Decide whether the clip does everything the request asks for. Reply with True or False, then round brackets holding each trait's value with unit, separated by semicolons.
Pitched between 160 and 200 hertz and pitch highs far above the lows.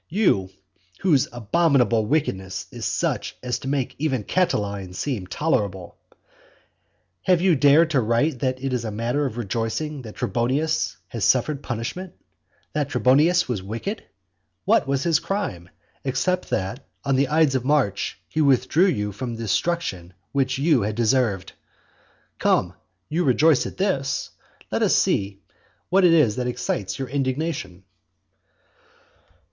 False (130 Hz; 5.9 semitones)